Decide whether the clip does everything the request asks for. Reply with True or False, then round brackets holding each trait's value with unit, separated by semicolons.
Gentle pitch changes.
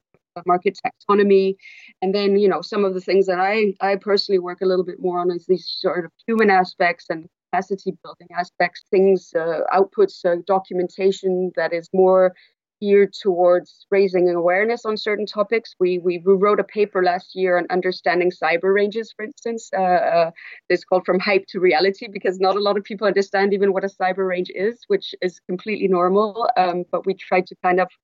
True (1.9 semitones)